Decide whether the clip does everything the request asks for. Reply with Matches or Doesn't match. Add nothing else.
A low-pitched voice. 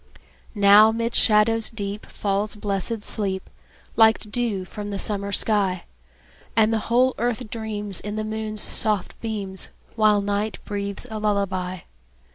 Doesn't match